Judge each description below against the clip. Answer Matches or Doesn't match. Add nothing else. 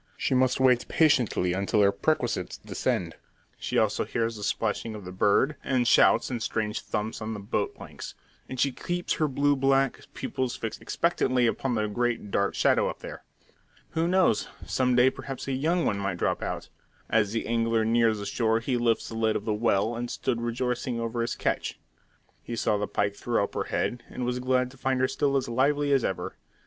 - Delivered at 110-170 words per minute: Doesn't match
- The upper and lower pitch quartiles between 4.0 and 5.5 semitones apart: Doesn't match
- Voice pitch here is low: Matches